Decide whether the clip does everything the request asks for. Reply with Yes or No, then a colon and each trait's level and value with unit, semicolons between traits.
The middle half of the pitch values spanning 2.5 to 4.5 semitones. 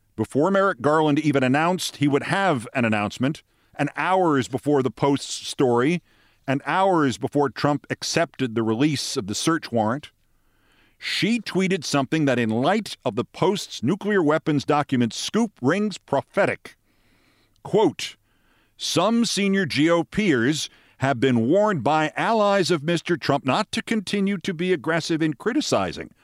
No: wide, 5.4 semitones